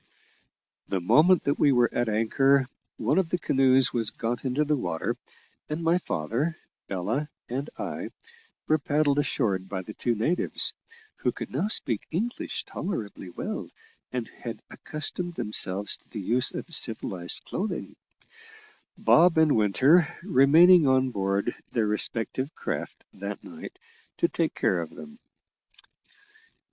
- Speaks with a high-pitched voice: No, low, 130 Hz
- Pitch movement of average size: No, wide, 6.6 semitones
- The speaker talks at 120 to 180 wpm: Yes, average, 140 wpm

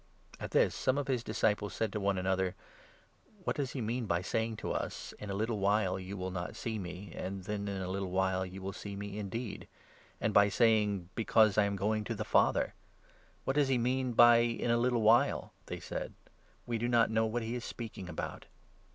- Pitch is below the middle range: Yes, low, 105 Hz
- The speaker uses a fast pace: Yes, fast, 240 wpm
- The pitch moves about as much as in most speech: Yes, average, 3.2 semitones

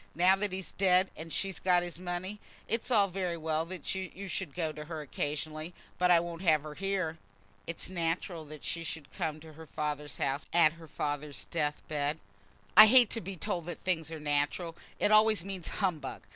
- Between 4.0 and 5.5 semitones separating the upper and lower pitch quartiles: No, average, 3.3 semitones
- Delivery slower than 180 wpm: No, average, 200 wpm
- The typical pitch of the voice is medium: Yes, medium, 170 Hz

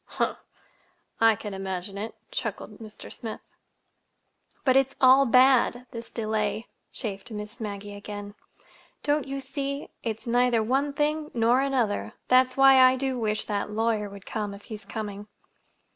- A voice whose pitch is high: Yes, high, 225 Hz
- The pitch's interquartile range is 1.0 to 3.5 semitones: No, average, 3.9 semitones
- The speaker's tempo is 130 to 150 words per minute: Yes, average, 145 wpm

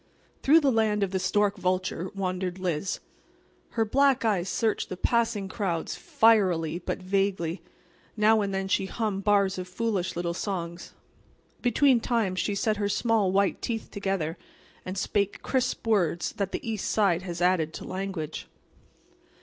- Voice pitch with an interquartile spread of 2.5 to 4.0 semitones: Yes, average, 3.0 semitones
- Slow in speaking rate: No, average, 155 wpm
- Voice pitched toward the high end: Yes, high, 195 Hz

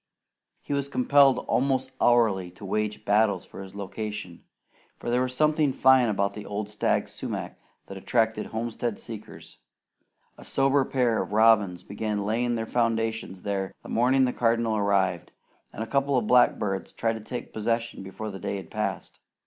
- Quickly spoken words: No, average, 165 wpm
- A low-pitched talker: Yes, low, 110 Hz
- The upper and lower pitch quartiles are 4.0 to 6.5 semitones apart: No, average, 3.4 semitones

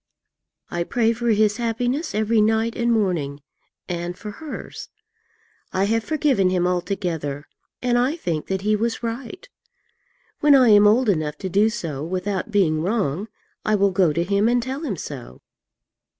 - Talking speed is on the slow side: No, average, 165 wpm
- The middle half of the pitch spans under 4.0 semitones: No, average, 4.8 semitones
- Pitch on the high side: Yes, high, 205 Hz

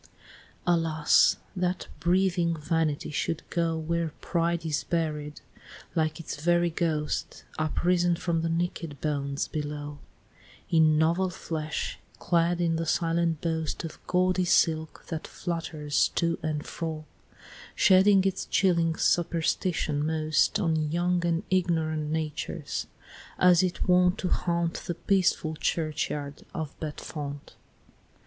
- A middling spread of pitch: No, narrow, 2.0 semitones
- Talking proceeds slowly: Yes, slow, 120 wpm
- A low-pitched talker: No, medium, 165 Hz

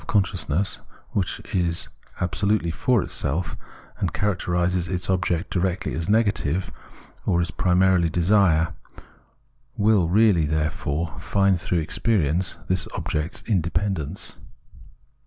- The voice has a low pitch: Yes, very low, 90 Hz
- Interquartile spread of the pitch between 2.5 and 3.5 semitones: Yes, average, 2.9 semitones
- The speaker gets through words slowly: Yes, slow, 110 wpm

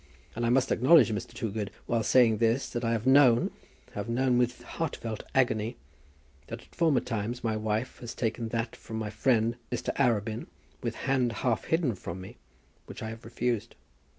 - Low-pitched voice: Yes, low, 115 Hz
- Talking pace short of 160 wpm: No, average, 180 wpm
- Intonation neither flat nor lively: No, narrow, 2.1 semitones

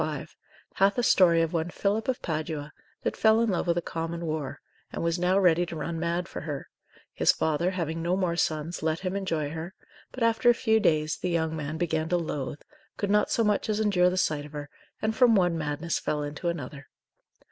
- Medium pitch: Yes, medium, 170 Hz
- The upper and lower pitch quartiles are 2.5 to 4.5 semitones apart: Yes, average, 3.4 semitones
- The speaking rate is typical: No, fast, 220 wpm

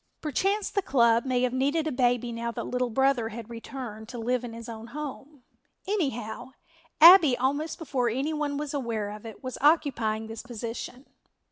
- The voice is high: Yes, very high, 250 Hz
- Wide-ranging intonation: No, average, 3.7 semitones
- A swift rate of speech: No, average, 175 wpm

